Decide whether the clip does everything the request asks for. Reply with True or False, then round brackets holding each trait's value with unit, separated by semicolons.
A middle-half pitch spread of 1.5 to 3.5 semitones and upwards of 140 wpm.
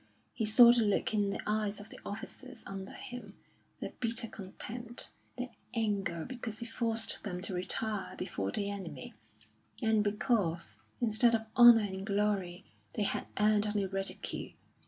True (2.6 semitones; 155 wpm)